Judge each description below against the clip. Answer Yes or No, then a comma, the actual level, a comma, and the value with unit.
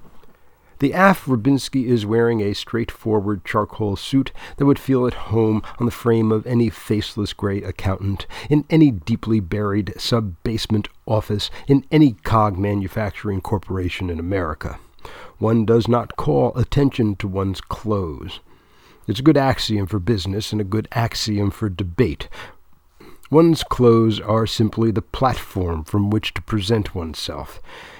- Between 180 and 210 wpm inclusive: No, average, 140 wpm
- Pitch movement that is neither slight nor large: Yes, average, 3.2 semitones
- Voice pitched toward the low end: Yes, low, 110 Hz